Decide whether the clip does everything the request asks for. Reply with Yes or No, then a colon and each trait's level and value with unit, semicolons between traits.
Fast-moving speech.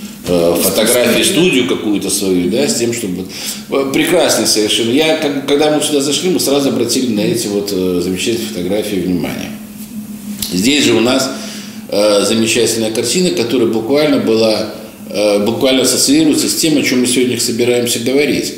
No: average, 140 wpm